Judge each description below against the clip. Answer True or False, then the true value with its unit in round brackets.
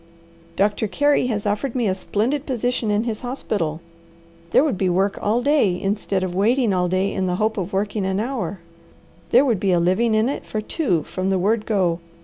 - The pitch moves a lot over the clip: False (4.0 semitones)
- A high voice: True (205 Hz)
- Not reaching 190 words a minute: False (205 wpm)